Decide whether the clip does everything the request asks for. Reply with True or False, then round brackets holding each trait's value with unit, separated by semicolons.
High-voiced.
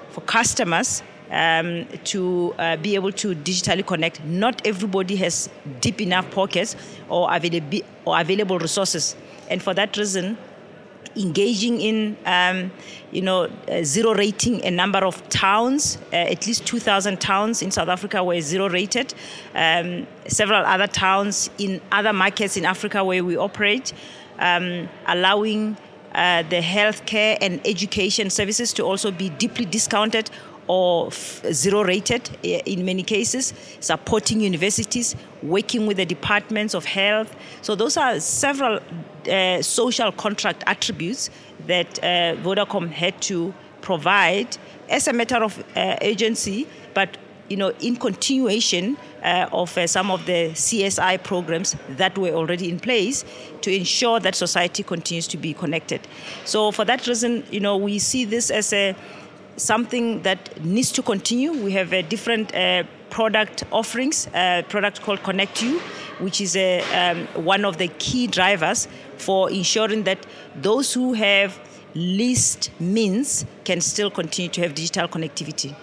True (195 Hz)